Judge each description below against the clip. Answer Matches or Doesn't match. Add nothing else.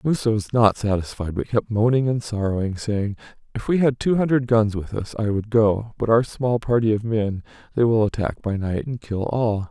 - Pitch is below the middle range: Matches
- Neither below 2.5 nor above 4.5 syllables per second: Doesn't match